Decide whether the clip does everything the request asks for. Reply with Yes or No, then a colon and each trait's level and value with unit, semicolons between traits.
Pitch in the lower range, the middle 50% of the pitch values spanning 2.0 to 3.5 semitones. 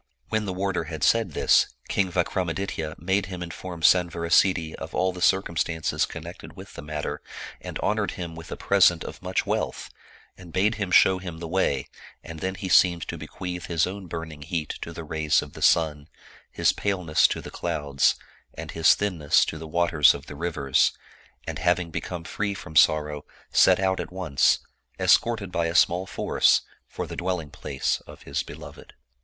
Yes: very low, 85 Hz; average, 2.8 semitones